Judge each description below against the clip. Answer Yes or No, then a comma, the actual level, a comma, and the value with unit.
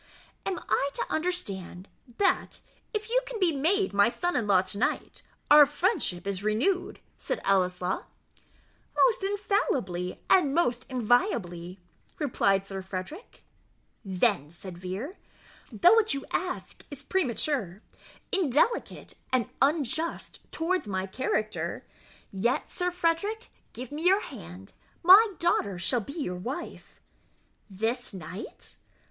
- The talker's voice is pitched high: Yes, very high, 255 Hz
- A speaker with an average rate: No, slow, 125 wpm